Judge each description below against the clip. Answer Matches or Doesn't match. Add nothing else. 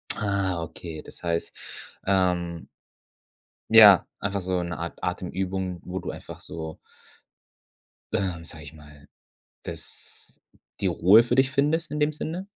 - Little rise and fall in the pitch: Doesn't match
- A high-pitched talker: Doesn't match